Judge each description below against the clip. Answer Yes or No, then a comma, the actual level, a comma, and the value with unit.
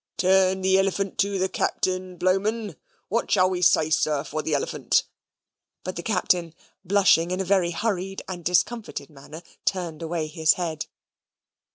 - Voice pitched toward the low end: No, medium, 185 Hz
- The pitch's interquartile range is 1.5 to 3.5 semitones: Yes, narrow, 2.6 semitones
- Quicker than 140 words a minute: Yes, average, 155 wpm